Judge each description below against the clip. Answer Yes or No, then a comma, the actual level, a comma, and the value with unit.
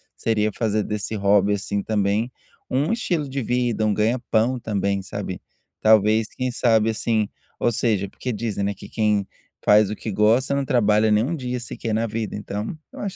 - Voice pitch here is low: Yes, low, 110 Hz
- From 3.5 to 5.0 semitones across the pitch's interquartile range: No, average, 2.7 semitones